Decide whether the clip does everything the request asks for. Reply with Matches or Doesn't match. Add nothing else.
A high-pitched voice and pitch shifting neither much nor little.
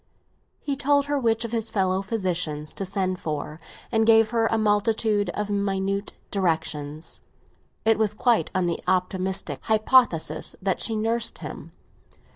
Matches